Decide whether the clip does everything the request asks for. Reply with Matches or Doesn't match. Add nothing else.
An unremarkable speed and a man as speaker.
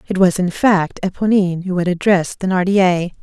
Doesn't match